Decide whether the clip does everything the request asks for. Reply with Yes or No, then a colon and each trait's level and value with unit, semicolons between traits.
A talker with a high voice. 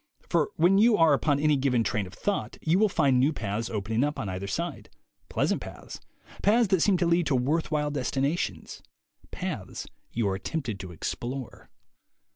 No: medium, 140 Hz